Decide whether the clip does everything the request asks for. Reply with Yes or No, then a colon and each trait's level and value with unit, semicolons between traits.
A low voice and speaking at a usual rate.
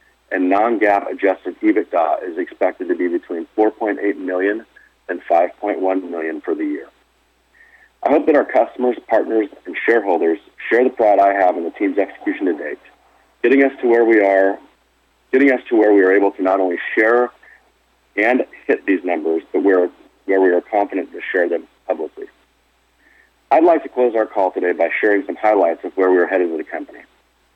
Yes: low, 110 Hz; average, 185 wpm